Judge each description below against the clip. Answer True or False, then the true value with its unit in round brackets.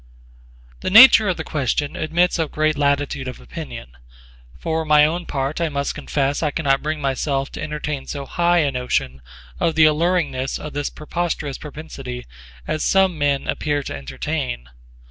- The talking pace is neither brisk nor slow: True (165 wpm)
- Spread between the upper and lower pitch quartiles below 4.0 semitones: True (2.7 semitones)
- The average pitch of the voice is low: False (145 Hz)